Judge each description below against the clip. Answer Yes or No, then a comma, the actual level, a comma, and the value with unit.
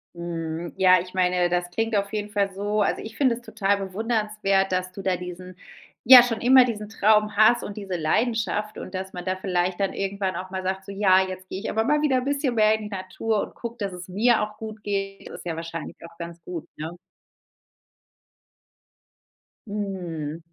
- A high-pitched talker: Yes, high, 195 Hz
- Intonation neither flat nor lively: Yes, average, 3.0 semitones